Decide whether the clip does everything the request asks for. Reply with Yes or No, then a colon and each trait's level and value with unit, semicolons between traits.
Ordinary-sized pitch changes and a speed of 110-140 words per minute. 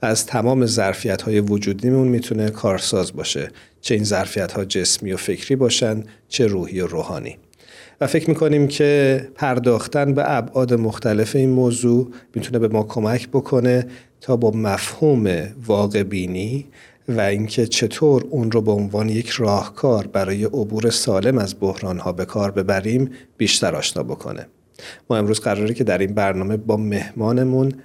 No: average, 3.7 semitones; average, 150 wpm